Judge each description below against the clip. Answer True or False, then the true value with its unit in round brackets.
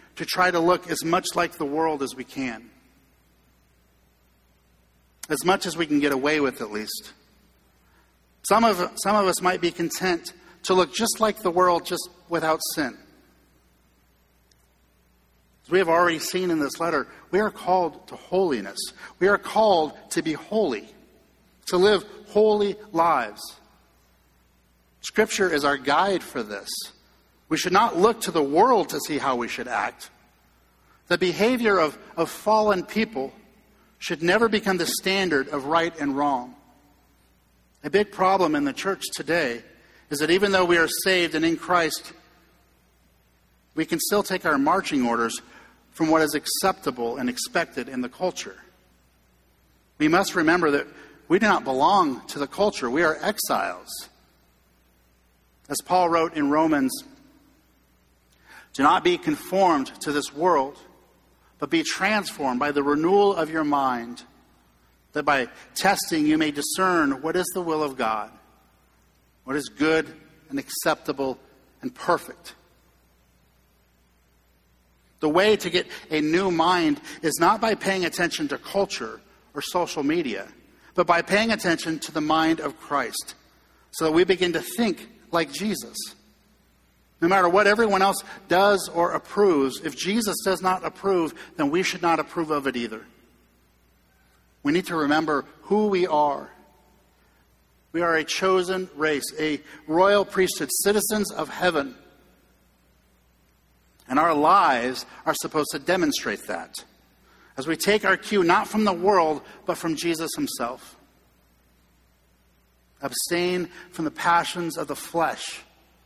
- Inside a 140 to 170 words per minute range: True (145 wpm)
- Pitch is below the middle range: False (165 Hz)